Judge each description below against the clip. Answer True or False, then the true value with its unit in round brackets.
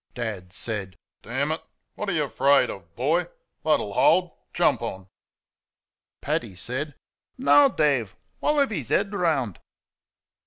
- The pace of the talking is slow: True (130 wpm)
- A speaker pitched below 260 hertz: True (140 Hz)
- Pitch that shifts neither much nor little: False (7.9 semitones)